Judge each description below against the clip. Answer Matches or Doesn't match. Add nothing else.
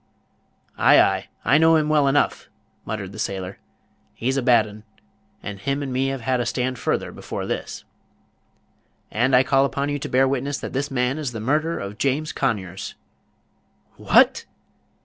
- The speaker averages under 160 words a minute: Doesn't match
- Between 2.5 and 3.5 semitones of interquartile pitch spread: Matches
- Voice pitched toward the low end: Matches